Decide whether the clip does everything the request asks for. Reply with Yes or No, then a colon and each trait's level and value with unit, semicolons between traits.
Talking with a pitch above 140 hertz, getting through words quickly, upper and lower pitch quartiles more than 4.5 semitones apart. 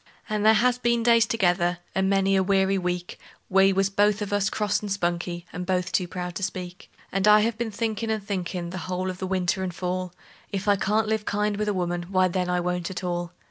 No: high, 190 Hz; fast, 235 wpm; narrow, 2.6 semitones